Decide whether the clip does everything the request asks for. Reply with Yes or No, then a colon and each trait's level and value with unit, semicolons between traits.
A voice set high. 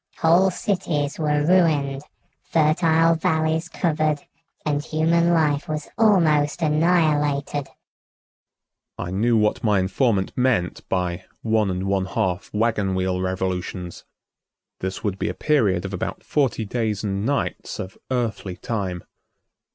No: low, 135 Hz